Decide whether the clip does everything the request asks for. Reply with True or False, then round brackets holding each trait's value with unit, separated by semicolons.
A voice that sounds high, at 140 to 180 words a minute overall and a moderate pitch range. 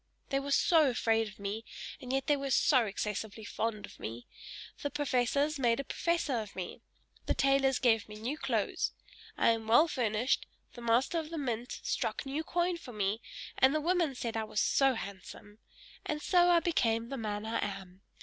False (245 Hz; 190 wpm; 4.6 semitones)